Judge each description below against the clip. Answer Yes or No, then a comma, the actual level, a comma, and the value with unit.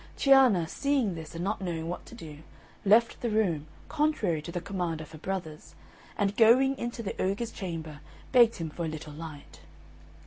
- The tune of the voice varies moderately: No, wide, 6.2 semitones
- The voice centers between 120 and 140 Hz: No, medium, 185 Hz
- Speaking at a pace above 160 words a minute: Yes, average, 180 wpm